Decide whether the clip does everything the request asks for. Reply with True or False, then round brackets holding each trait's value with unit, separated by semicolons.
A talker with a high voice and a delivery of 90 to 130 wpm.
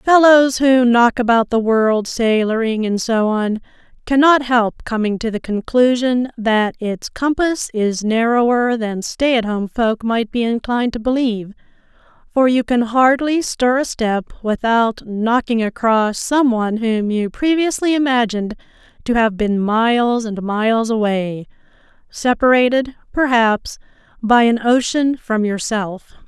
False (235 Hz; 140 wpm)